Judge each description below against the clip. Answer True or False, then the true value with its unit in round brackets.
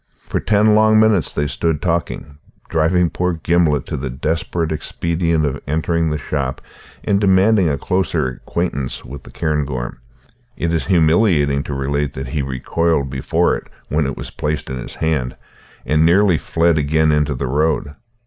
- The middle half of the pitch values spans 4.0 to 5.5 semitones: False (3.2 semitones)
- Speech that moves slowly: False (165 wpm)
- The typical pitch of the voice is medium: False (80 Hz)